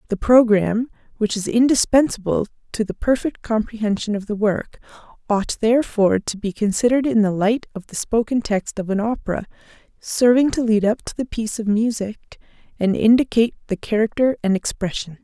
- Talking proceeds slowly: No, average, 165 wpm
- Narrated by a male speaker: No, female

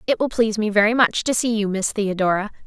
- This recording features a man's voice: No, female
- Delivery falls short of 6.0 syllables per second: No, 6.3 syllables/s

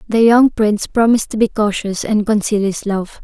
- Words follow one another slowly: No, fast, 205 wpm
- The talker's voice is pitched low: No, high, 215 Hz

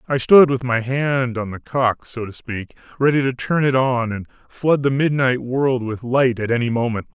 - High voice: No, low, 125 Hz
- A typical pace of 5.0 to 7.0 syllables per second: No, 4.7 syllables/s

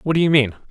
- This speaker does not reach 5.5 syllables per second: No, 7.4 syllables/s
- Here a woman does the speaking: No, male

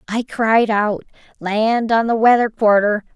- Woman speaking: Yes, female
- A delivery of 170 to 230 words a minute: No, average, 150 wpm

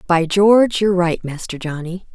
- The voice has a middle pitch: Yes, medium, 180 Hz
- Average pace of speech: Yes, average, 170 wpm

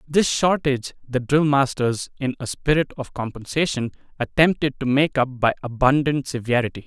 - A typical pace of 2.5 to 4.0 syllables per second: No, 5.1 syllables/s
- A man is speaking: Yes, male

